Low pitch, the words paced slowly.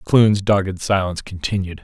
Yes: very low, 95 Hz; slow, 130 wpm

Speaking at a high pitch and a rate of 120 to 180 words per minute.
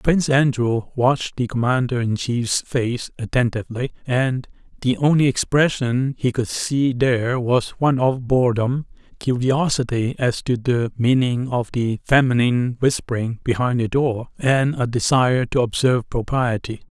No: low, 125 Hz; average, 140 wpm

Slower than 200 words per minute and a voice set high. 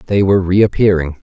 No: average, 140 wpm; very low, 95 Hz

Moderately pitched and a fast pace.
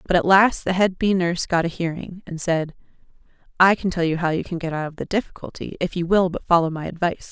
Yes: medium, 175 Hz; fast, 245 wpm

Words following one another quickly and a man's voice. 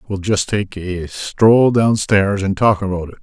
No: average, 185 wpm; male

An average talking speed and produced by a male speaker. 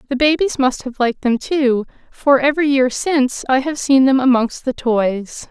No: average, 195 wpm; female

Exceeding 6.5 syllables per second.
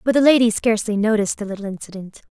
Yes: 7.5 syllables/s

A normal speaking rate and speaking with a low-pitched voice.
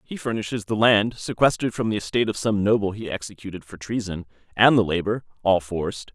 Yes: average, 165 wpm; low, 105 Hz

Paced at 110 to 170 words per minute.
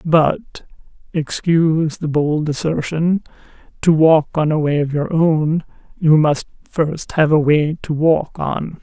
Yes: average, 150 wpm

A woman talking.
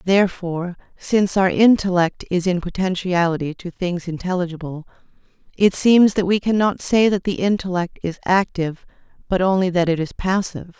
Yes: female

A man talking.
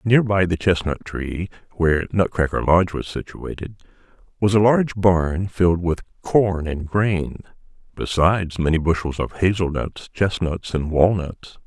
Yes: male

